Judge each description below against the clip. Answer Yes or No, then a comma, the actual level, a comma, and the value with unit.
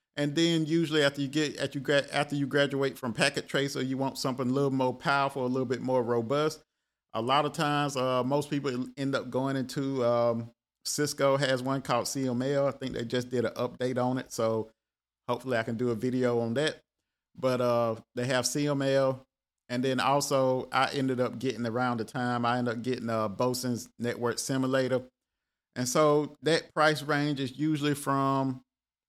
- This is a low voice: Yes, low, 130 Hz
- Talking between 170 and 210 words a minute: Yes, average, 185 wpm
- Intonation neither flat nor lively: No, narrow, 2.3 semitones